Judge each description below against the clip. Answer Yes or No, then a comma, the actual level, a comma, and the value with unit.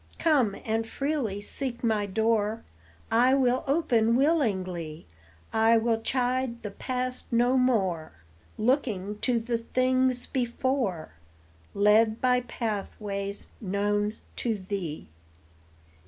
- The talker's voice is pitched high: Yes, high, 230 Hz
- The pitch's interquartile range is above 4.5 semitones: No, average, 3.7 semitones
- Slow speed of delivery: Yes, slow, 105 wpm